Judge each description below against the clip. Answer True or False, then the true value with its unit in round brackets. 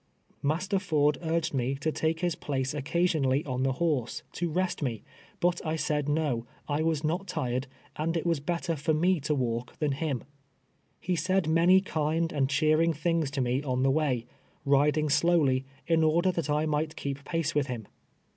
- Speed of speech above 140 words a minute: True (185 wpm)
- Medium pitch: True (155 Hz)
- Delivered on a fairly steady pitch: False (3.2 semitones)